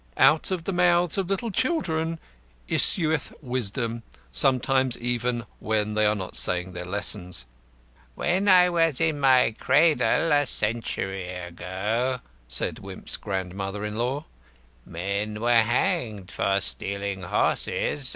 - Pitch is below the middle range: Yes, low, 120 Hz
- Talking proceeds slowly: Yes, slow, 125 wpm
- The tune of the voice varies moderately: No, wide, 8.1 semitones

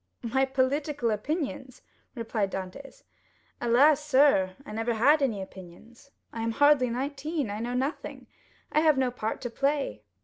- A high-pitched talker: Yes, very high, 255 Hz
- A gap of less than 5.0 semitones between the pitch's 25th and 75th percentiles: Yes, average, 4.1 semitones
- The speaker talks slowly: No, average, 145 wpm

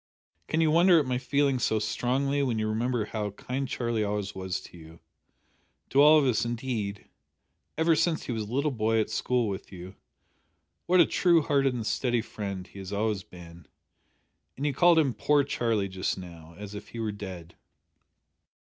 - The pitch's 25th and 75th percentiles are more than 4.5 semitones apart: Yes, wide, 5.5 semitones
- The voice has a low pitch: Yes, low, 115 Hz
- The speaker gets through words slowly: No, average, 185 wpm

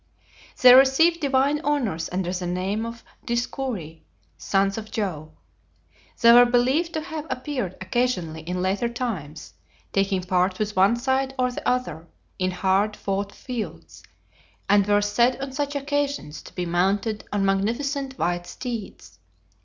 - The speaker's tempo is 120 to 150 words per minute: Yes, average, 145 wpm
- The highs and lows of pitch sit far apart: Yes, wide, 5.8 semitones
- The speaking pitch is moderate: No, high, 220 Hz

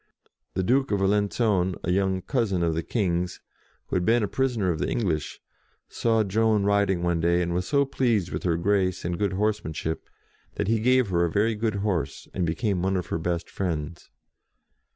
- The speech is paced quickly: No, average, 195 wpm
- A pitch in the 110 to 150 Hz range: No, very low, 95 Hz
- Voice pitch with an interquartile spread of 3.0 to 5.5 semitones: Yes, average, 3.8 semitones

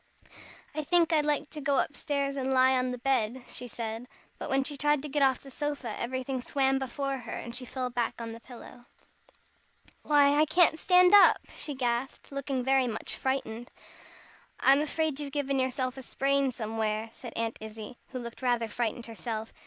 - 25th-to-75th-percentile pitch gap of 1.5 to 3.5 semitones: Yes, average, 2.9 semitones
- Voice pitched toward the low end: No, very high, 265 Hz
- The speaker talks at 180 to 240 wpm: Yes, average, 190 wpm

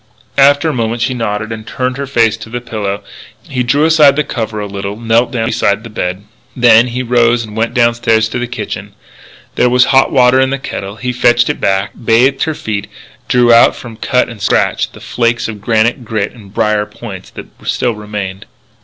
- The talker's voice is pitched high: No, low, 115 Hz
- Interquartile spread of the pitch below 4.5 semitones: Yes, narrow, 2.6 semitones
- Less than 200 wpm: No, fast, 205 wpm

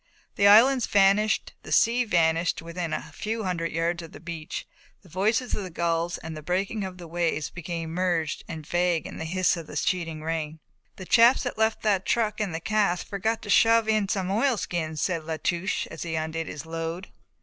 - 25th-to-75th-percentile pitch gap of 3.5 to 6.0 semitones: Yes, average, 4.0 semitones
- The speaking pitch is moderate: Yes, medium, 175 Hz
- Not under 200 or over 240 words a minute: Yes, fast, 205 wpm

